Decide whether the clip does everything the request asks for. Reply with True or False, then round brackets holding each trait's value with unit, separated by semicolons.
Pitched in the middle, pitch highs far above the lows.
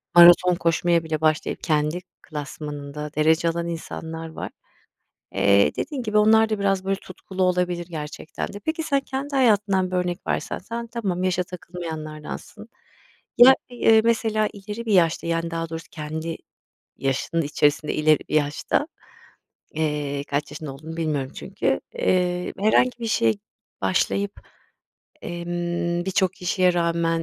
False (170 Hz; 3.9 semitones)